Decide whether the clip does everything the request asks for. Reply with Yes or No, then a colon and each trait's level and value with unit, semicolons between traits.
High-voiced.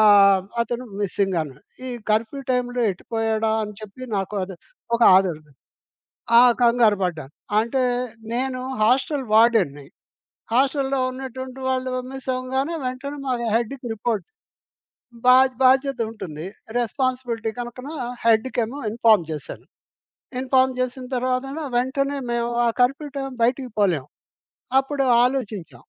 Yes: high, 245 Hz